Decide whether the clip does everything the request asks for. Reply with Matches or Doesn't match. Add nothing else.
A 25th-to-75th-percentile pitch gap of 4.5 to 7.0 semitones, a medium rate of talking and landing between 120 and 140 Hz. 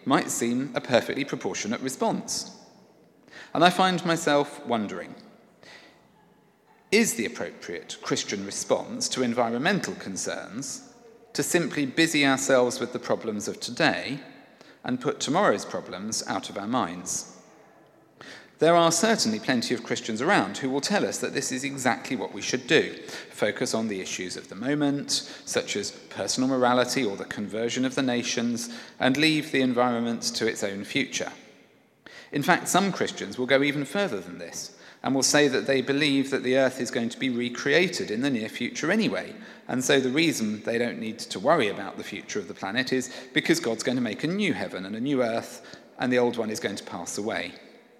Matches